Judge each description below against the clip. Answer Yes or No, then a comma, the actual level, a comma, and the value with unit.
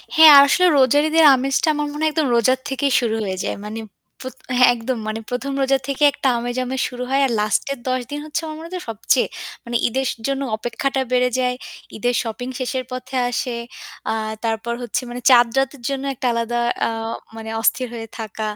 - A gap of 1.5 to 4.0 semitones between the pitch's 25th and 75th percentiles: Yes, narrow, 2.6 semitones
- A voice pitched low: No, very high, 255 Hz